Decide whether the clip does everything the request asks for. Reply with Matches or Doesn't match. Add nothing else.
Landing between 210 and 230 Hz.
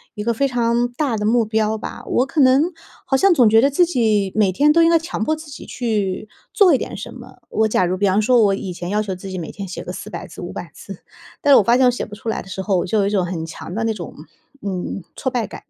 Matches